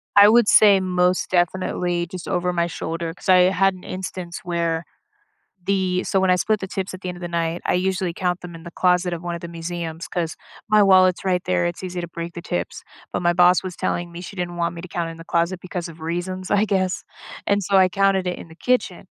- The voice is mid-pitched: Yes, medium, 180 Hz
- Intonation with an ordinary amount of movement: No, narrow, 1.6 semitones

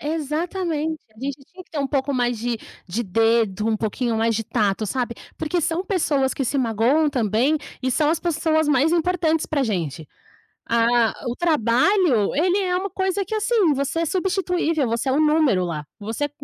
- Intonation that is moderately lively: No, wide, 6.3 semitones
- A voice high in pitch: Yes, very high, 280 Hz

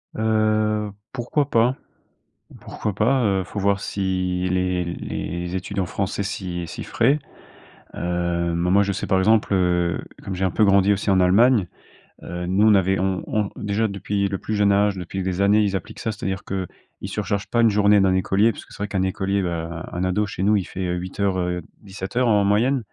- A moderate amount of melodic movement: No, narrow, 2.3 semitones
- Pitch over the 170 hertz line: No, low, 100 Hz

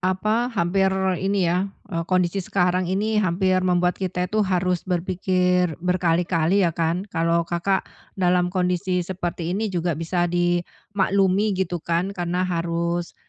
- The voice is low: No, medium, 180 Hz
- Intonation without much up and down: Yes, narrow, 1.6 semitones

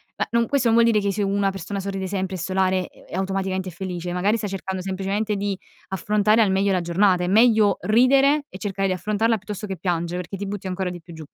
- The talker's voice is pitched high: Yes, high, 195 Hz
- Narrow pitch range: Yes, narrow, 2.1 semitones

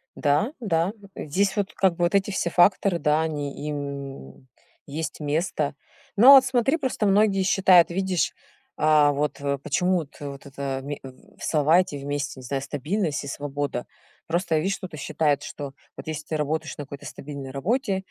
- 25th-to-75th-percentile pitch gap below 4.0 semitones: No, average, 4.9 semitones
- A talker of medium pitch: Yes, medium, 155 Hz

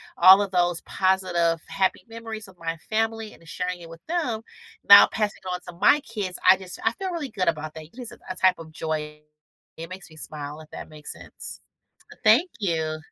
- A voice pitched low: No, medium, 185 Hz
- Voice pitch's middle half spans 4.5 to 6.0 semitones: Yes, average, 4.8 semitones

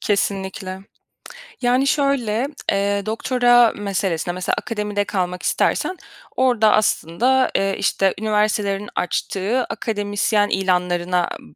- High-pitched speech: Yes, high, 205 Hz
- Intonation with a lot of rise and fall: No, average, 3.3 semitones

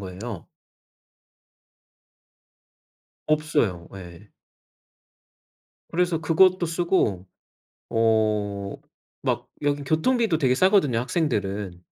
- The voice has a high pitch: No, low, 125 Hz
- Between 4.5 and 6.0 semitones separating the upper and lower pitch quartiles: No, wide, 8.5 semitones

